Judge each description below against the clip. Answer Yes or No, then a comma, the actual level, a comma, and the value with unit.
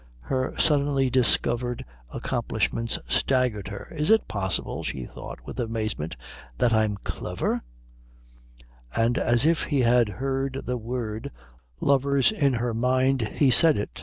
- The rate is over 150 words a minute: No, slow, 135 wpm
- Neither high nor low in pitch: No, low, 125 Hz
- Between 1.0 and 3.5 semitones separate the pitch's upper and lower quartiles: Yes, average, 3.2 semitones